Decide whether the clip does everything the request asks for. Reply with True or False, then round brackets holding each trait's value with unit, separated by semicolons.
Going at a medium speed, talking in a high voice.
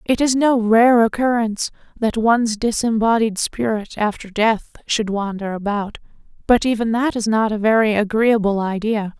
True (150 wpm; 220 Hz)